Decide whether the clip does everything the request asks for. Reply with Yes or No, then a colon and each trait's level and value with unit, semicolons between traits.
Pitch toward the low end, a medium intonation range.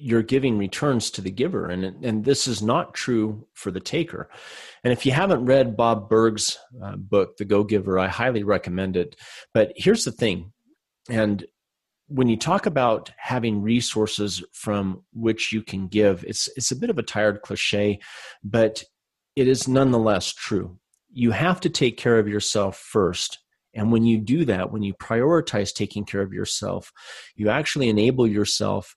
Yes: low, 110 Hz; average, 3.1 semitones